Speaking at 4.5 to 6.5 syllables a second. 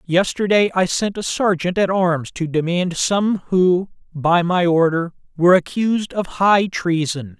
No: 4.2 syllables/s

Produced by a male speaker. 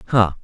Yes: male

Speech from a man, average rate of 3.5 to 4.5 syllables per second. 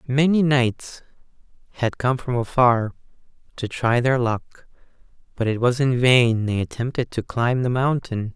Yes: male; 4.2 syllables/s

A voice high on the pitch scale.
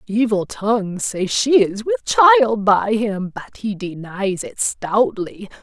Yes: high, 215 Hz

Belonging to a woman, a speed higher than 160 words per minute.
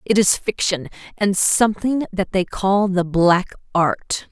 No: female; average, 155 wpm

